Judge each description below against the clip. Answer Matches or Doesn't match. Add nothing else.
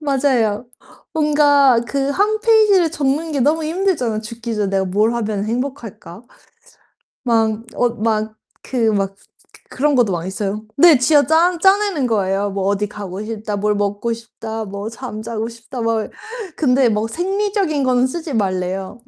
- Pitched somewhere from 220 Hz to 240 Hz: Matches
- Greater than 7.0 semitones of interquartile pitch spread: Doesn't match